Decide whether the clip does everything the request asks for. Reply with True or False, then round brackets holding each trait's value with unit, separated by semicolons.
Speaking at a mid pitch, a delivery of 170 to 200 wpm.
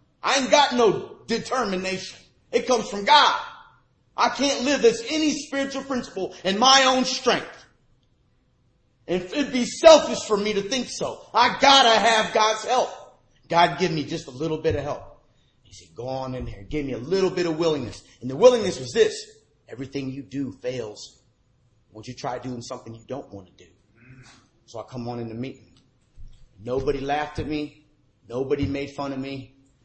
True (150 Hz; 185 wpm)